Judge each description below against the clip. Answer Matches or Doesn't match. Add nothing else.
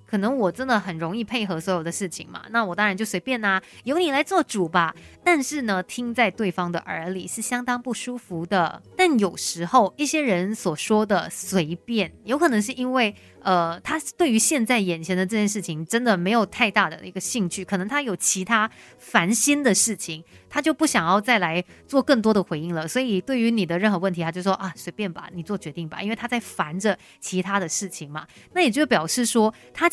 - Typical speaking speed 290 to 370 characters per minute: Matches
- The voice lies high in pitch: Matches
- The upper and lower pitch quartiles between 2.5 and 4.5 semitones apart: Doesn't match